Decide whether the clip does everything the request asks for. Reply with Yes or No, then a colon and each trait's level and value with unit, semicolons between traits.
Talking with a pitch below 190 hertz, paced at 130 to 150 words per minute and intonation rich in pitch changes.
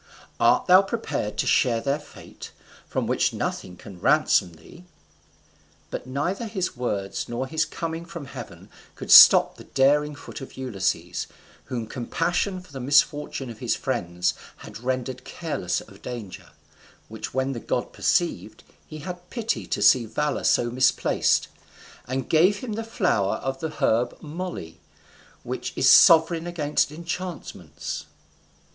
Yes: medium, 140 Hz; average, 145 wpm; wide, 6.1 semitones